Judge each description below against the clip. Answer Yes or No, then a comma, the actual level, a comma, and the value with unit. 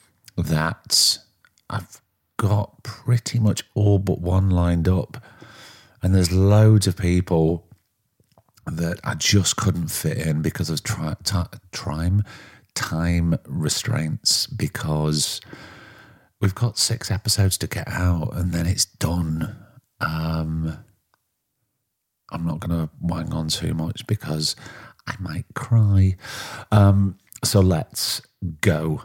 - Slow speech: Yes, slow, 115 wpm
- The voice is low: Yes, very low, 95 Hz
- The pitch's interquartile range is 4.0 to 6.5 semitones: Yes, average, 4.3 semitones